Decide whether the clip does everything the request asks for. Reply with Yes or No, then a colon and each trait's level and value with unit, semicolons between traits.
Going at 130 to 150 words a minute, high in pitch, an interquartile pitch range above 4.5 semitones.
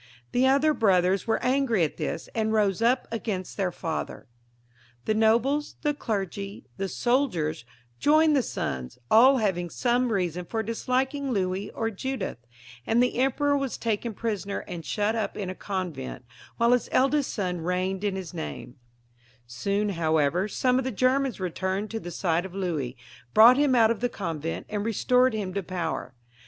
No: average, 170 wpm; high, 210 Hz; wide, 5.4 semitones